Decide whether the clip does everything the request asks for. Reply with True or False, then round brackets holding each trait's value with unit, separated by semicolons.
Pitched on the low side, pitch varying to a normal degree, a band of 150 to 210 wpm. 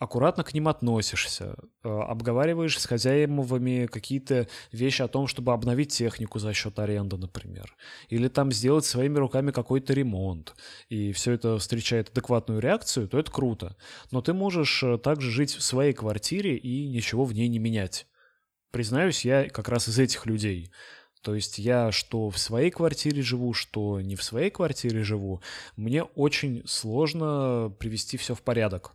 True (120 Hz; 3.8 semitones; 160 wpm)